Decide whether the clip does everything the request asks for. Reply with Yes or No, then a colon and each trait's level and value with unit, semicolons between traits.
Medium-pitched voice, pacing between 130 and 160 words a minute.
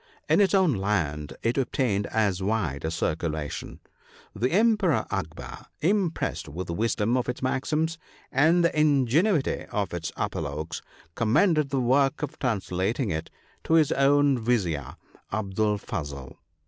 No: low, 115 Hz; average, 145 wpm